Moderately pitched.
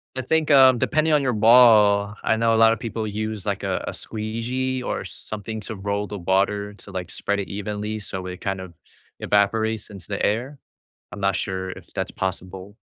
No: low, 105 Hz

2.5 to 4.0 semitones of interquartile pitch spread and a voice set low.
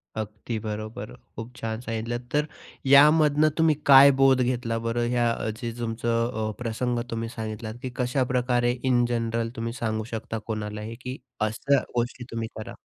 No: narrow, 2.1 semitones; low, 120 Hz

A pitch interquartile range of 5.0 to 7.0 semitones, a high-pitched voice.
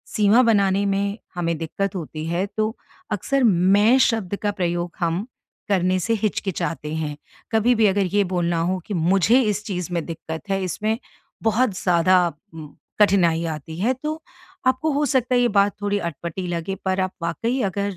No: average, 4.0 semitones; high, 195 Hz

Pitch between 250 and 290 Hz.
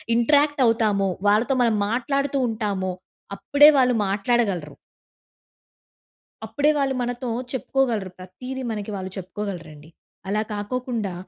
No: high, 225 Hz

